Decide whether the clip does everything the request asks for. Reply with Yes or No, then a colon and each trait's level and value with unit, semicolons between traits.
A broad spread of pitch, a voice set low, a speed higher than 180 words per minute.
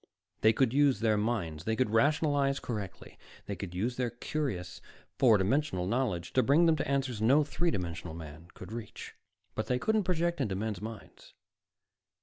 No: wide, 6.0 semitones; low, 115 Hz; average, 170 wpm